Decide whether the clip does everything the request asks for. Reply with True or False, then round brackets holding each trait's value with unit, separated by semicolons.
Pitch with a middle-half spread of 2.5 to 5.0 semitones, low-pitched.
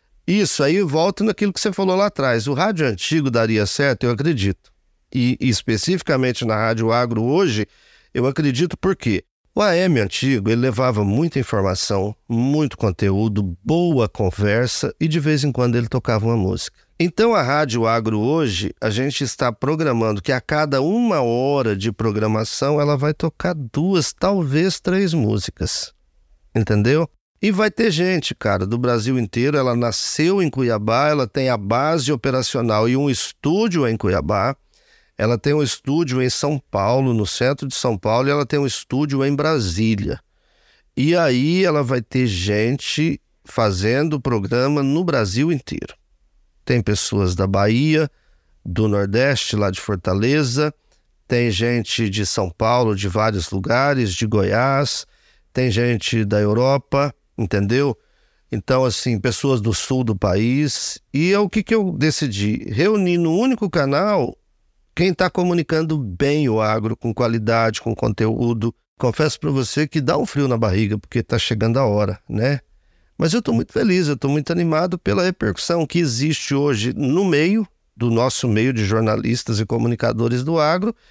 False (5.4 semitones; 125 Hz)